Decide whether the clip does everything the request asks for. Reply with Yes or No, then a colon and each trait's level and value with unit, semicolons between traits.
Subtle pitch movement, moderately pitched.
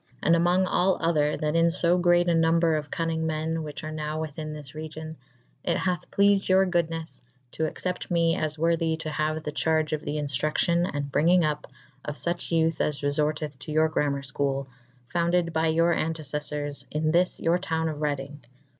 Yes: narrow, 2.0 semitones; medium, 160 Hz